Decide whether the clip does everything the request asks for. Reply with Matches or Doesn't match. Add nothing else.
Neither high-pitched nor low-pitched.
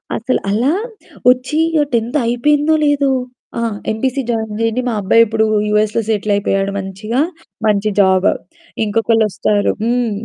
Doesn't match